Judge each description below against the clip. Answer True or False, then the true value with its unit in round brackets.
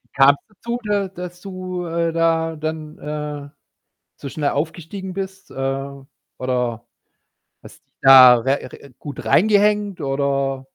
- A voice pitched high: False (155 Hz)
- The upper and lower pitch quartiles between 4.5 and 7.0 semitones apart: True (5.1 semitones)